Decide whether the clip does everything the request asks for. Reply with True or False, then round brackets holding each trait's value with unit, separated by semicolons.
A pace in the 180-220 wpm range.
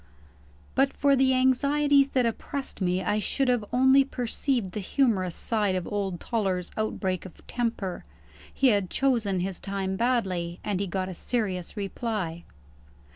False (150 wpm)